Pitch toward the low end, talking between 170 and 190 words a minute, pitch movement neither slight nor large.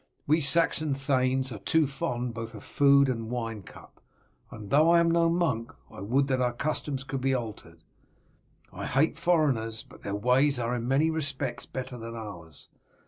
Yes: low, 130 Hz; average, 180 wpm; average, 4.1 semitones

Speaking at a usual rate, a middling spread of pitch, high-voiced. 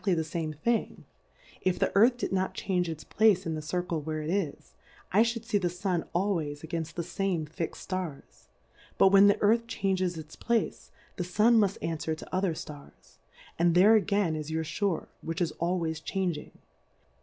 No: average, 190 wpm; average, 3.7 semitones; medium, 180 Hz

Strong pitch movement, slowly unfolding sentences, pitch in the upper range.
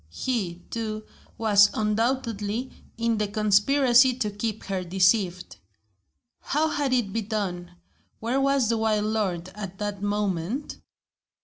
No: average, 3.0 semitones; slow, 125 wpm; high, 215 Hz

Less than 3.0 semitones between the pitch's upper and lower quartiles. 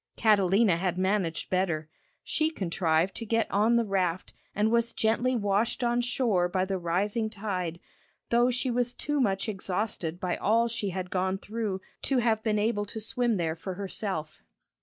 No: average, 4.0 semitones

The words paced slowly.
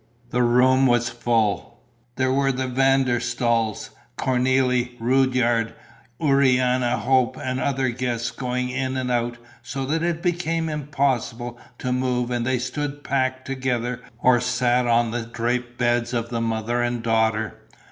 No: average, 145 wpm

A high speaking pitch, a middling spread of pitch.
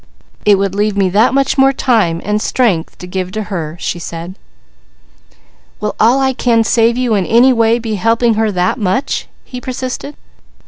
Yes: high, 220 Hz; average, 4.5 semitones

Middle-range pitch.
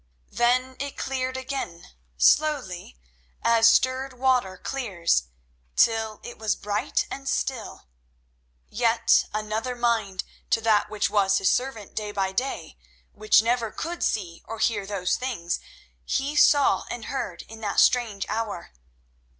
No: high, 225 Hz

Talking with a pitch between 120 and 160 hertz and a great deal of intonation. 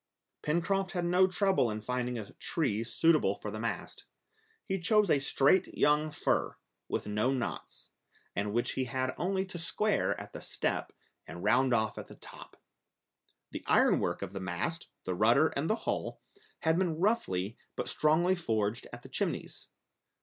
Yes: medium, 140 Hz; wide, 8.2 semitones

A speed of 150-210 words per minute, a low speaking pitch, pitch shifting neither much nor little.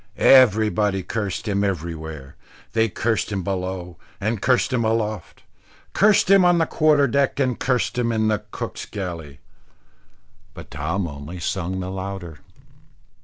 No: average, 140 wpm; low, 100 Hz; average, 4.6 semitones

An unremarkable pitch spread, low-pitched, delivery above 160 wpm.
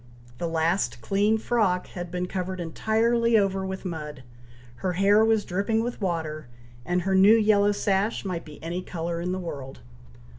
No: average, 3.5 semitones; medium, 185 Hz; average, 170 wpm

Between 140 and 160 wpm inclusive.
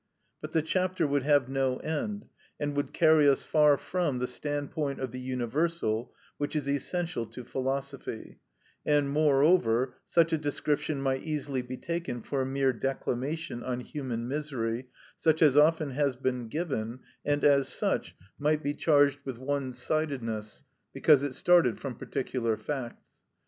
Yes: average, 155 wpm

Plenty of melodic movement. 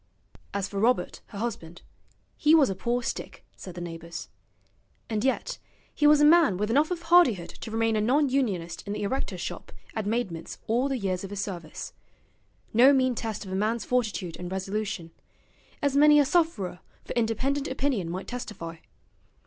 Yes: wide, 6.0 semitones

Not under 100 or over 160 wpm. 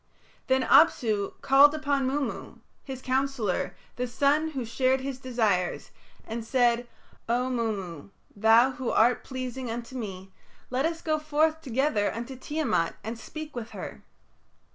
Yes: average, 140 wpm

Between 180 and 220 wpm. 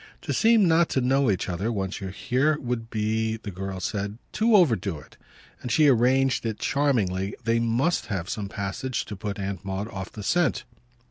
Yes: average, 195 wpm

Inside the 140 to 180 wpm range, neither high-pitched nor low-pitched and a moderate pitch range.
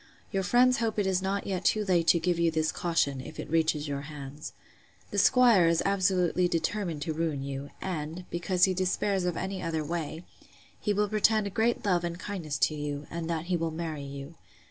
No: fast, 205 wpm; medium, 170 Hz; average, 3.6 semitones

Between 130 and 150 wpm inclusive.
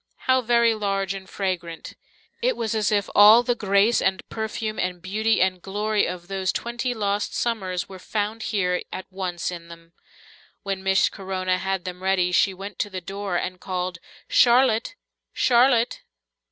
No: average, 165 wpm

